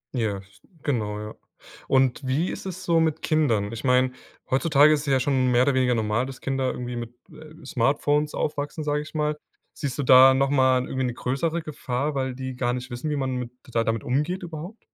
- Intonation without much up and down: No, average, 3.2 semitones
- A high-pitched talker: No, low, 130 Hz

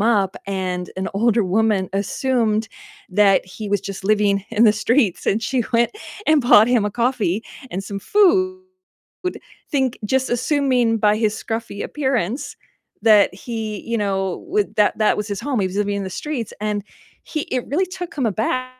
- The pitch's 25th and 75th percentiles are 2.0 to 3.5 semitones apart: No, average, 4.0 semitones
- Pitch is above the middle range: Yes, high, 220 Hz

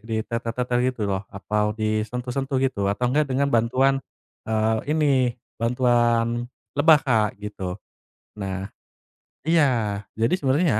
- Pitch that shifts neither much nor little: Yes, average, 3.7 semitones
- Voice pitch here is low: Yes, low, 120 Hz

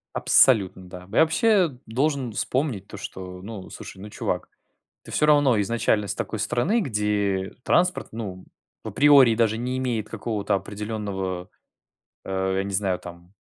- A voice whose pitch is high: No, low, 105 Hz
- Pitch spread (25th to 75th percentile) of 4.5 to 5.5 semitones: Yes, average, 5.0 semitones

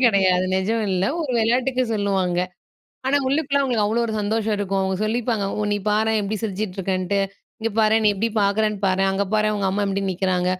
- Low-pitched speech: No, high, 210 Hz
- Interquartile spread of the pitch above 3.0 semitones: No, narrow, 2.5 semitones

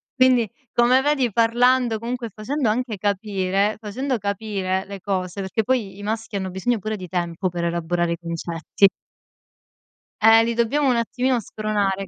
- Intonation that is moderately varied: Yes, average, 4.0 semitones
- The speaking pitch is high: Yes, high, 215 Hz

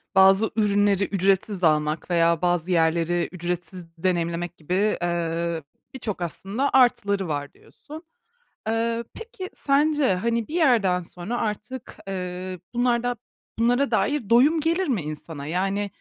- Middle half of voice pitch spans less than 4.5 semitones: No, wide, 5.4 semitones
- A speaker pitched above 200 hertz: No, high, 195 Hz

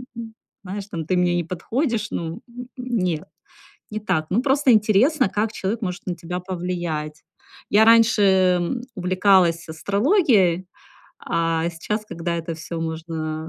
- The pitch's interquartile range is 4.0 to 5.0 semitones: Yes, average, 4.7 semitones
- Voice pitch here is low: No, medium, 185 Hz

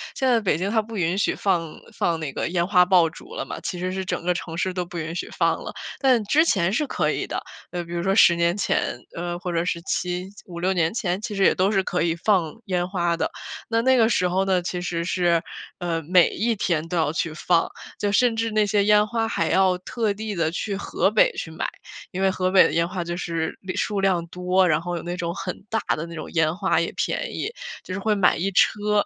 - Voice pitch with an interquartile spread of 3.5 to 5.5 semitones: No, average, 2.9 semitones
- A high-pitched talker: No, medium, 180 Hz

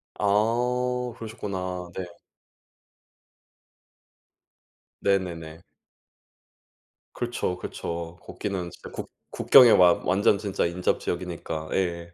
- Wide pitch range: No, average, 4.0 semitones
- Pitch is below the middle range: Yes, very low, 95 Hz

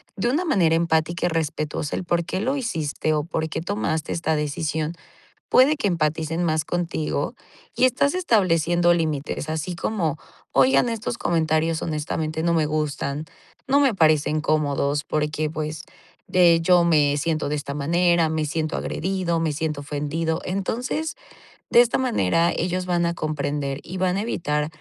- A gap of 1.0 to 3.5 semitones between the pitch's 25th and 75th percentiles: Yes, average, 2.8 semitones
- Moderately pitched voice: Yes, medium, 160 Hz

